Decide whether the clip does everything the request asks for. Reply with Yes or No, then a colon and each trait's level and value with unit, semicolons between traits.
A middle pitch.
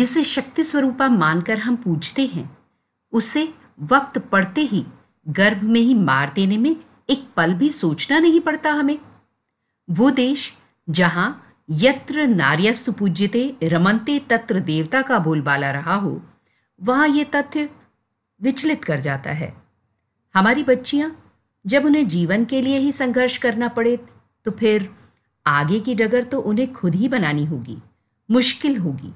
No: high, 230 Hz